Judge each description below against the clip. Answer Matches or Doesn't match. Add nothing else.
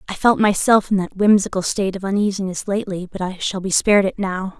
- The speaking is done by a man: Doesn't match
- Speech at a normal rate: Doesn't match